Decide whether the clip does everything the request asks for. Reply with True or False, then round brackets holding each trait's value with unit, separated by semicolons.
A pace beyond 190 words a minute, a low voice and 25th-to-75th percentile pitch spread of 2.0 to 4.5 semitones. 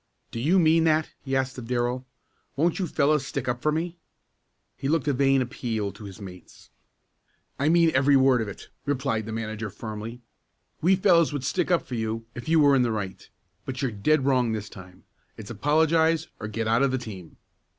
False (200 wpm; 130 Hz; 5.3 semitones)